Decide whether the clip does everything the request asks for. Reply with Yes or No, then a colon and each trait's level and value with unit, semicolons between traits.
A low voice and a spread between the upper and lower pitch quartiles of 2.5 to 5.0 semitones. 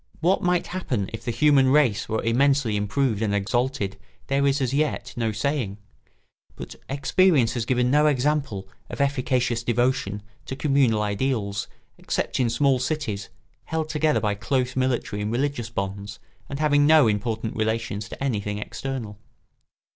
Yes: low, 125 Hz; average, 4.6 semitones